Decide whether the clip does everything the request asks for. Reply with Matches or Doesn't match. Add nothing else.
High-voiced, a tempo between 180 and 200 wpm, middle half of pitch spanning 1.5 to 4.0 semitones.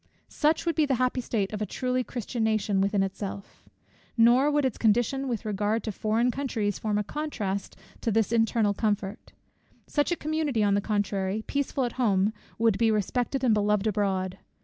Matches